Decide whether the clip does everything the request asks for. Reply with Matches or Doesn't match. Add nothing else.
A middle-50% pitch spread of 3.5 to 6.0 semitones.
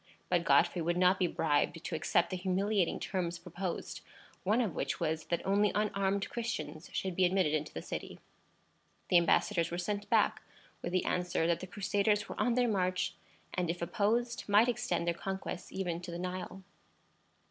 Doesn't match